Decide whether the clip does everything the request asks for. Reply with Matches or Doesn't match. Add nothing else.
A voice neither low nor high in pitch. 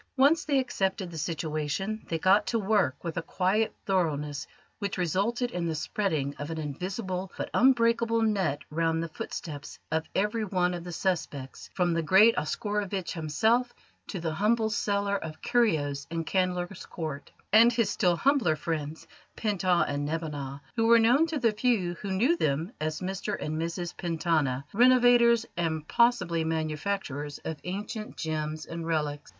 Matches